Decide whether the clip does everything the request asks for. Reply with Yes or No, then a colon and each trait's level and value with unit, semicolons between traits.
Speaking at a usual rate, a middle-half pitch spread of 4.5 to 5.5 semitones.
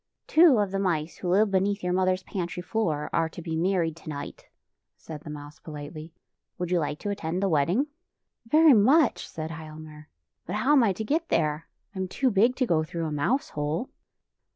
No: fast, 220 wpm; average, 4.9 semitones